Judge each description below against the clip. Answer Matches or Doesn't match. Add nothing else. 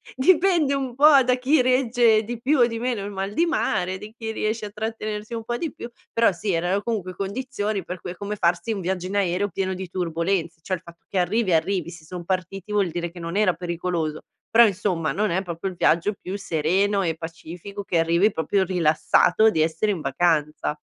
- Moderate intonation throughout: Matches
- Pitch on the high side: Matches